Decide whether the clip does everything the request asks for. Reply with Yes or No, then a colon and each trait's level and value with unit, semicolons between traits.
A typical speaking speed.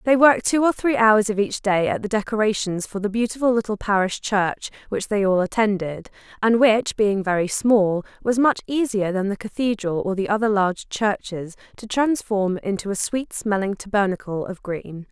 Yes: average, 185 wpm